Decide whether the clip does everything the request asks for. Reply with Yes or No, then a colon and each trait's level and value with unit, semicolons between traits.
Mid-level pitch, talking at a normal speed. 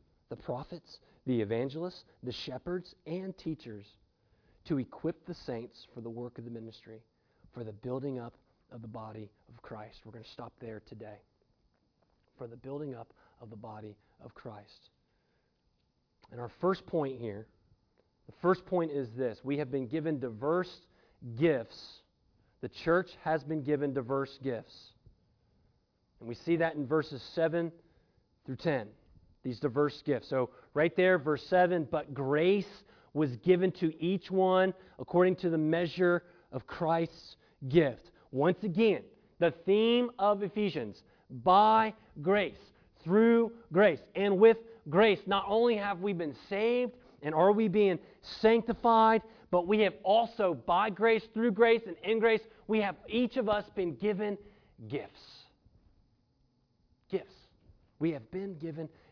Yes: medium, 160 Hz; average, 145 wpm